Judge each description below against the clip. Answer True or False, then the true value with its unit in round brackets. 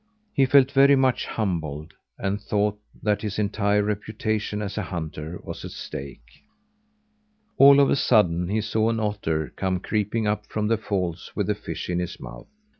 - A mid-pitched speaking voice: False (105 Hz)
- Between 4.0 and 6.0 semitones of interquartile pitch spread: False (3.5 semitones)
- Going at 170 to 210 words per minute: True (175 wpm)